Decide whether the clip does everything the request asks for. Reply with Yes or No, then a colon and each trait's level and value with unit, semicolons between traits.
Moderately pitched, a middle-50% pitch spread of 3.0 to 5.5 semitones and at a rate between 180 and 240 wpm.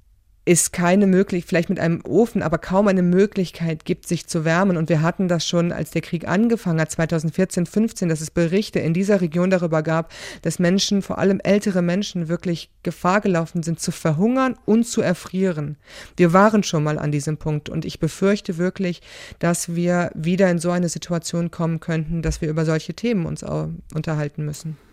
No: medium, 175 Hz; narrow, 2.6 semitones; fast, 190 wpm